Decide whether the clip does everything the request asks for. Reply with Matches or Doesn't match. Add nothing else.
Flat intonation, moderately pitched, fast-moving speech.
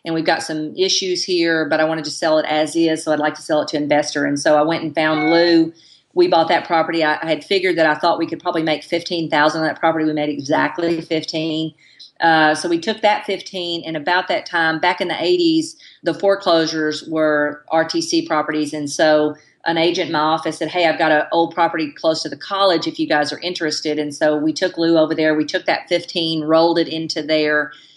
Matches